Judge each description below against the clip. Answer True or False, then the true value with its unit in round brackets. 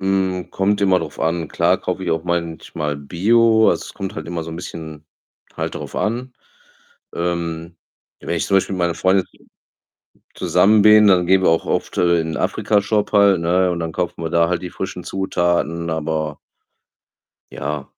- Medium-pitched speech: False (85 Hz)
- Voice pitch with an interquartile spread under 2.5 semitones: False (2.8 semitones)